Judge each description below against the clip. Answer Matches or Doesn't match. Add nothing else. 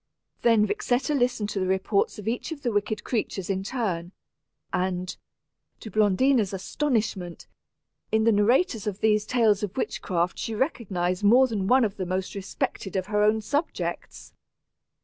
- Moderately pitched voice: Doesn't match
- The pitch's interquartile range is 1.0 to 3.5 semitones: Doesn't match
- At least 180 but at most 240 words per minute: Doesn't match